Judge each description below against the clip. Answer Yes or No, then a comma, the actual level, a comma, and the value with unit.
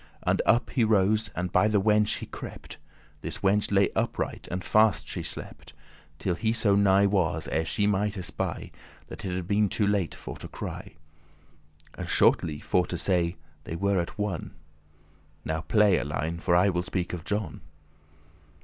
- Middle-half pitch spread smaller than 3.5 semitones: Yes, average, 3.0 semitones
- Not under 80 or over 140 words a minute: No, average, 175 wpm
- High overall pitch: No, very low, 95 Hz